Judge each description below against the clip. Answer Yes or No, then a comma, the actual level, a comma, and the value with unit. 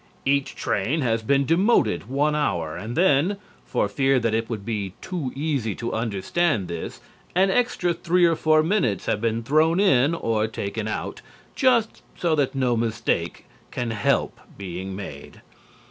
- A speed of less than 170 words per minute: Yes, average, 160 wpm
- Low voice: Yes, low, 130 Hz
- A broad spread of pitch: Yes, wide, 7.0 semitones